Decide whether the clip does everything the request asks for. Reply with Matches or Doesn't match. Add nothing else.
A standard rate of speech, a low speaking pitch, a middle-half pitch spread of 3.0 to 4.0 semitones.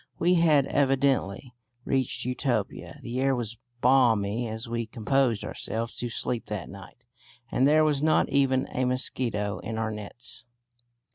Matches